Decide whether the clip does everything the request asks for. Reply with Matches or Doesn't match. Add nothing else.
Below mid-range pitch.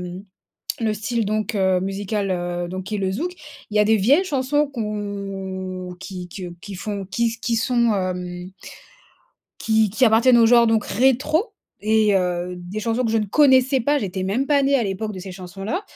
Doesn't match